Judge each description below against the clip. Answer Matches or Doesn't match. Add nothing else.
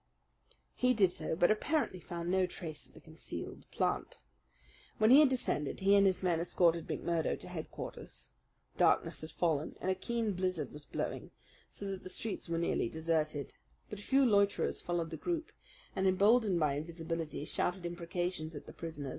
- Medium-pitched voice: Matches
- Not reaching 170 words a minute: Doesn't match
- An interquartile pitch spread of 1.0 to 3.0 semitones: Doesn't match